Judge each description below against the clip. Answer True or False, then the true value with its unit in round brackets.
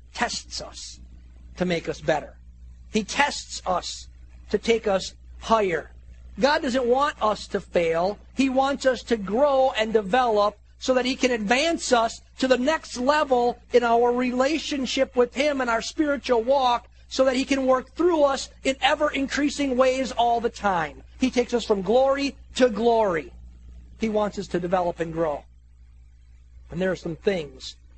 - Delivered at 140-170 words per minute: True (165 wpm)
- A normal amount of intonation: False (8.0 semitones)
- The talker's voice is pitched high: True (235 Hz)